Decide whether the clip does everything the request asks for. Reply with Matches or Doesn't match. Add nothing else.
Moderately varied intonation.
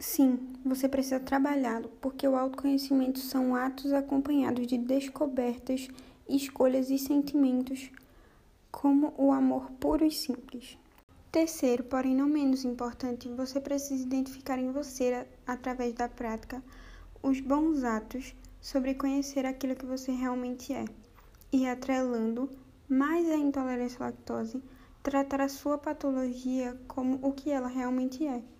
Doesn't match